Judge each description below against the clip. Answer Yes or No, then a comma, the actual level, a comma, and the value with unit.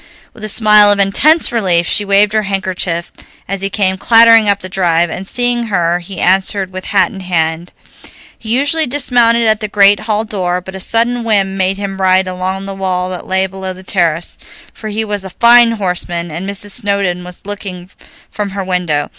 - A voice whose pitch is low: No, high, 195 Hz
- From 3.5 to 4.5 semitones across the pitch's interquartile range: No, average, 2.7 semitones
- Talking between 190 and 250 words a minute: Yes, average, 195 wpm